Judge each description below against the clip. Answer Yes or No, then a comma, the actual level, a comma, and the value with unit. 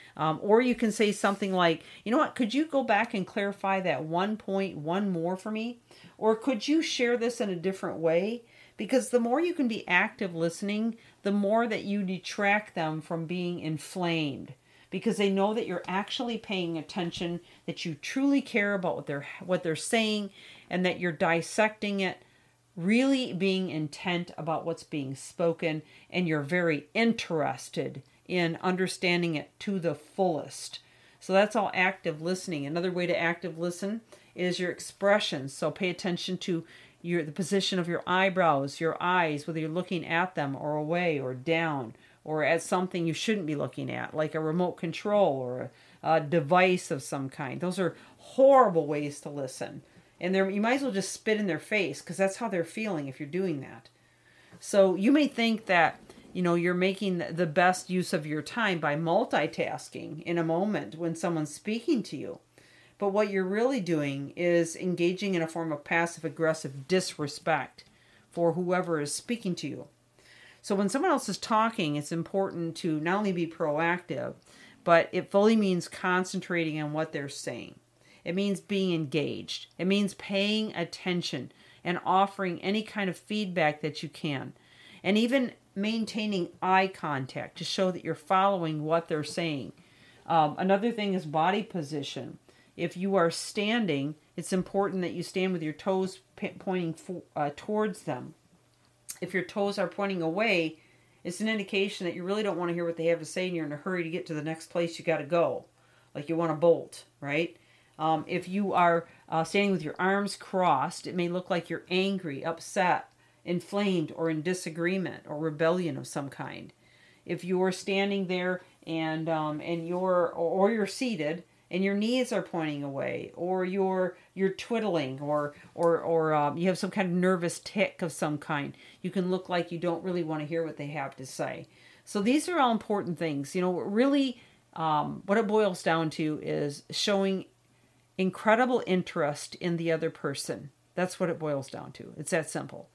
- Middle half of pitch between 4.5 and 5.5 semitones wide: No, average, 3.4 semitones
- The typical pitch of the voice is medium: Yes, medium, 180 Hz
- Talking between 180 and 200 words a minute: Yes, average, 185 wpm